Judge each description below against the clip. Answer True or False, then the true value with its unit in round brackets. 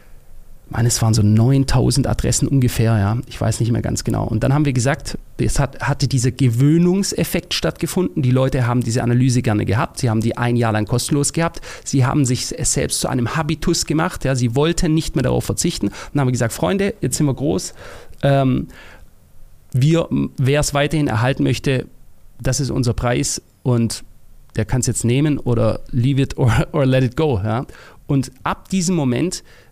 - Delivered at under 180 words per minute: False (190 wpm)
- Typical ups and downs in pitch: True (3.7 semitones)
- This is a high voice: False (130 Hz)